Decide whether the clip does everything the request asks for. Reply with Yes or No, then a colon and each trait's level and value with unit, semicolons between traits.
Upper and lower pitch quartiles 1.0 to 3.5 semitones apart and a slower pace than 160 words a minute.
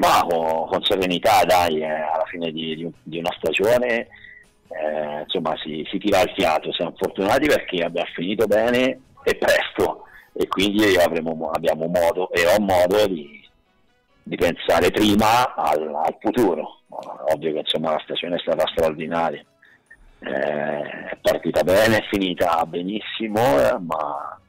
Yes: narrow, 2.6 semitones; average, 145 wpm